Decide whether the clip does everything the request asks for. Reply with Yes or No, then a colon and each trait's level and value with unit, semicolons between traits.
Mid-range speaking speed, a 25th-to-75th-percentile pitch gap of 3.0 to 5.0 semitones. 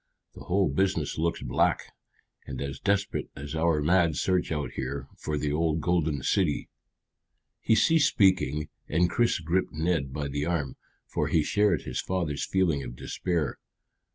Yes: average, 155 wpm; average, 4.1 semitones